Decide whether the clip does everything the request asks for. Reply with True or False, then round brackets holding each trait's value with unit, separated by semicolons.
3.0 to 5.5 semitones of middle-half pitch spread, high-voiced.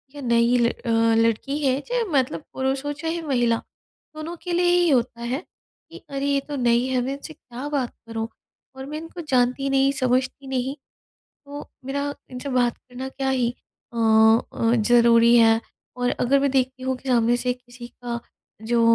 False (2.6 semitones; 255 Hz)